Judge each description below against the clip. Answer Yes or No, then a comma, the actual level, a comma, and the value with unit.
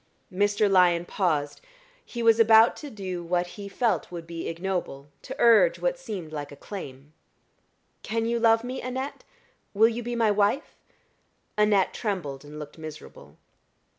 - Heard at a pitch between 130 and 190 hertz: No, high, 200 Hz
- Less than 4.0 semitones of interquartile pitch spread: No, average, 5.3 semitones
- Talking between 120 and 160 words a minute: Yes, average, 155 wpm